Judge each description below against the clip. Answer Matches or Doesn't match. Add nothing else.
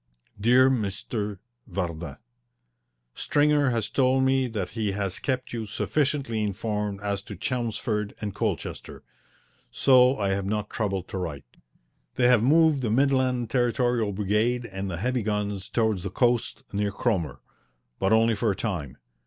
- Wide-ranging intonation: Doesn't match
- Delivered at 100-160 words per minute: Matches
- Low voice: Matches